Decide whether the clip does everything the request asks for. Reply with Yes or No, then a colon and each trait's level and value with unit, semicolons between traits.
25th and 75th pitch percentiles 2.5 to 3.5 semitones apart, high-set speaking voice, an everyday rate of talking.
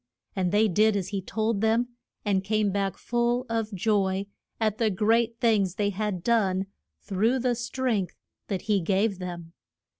Yes: average, 2.9 semitones; high, 210 Hz; average, 160 wpm